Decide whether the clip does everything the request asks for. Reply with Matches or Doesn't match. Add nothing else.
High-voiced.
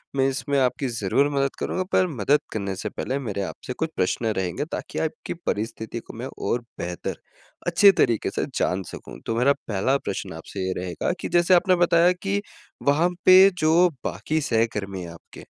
Doesn't match